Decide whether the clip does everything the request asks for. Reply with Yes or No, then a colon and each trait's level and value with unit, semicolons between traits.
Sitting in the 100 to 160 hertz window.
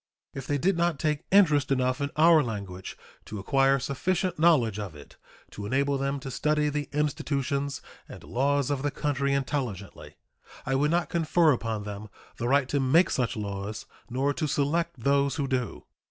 Yes: medium, 140 Hz